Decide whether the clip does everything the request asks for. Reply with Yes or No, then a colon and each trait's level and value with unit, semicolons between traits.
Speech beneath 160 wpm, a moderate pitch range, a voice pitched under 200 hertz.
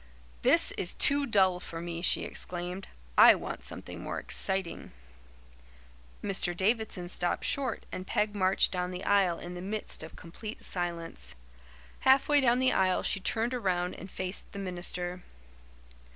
Yes: average, 150 wpm; average, 3.0 semitones; medium, 185 Hz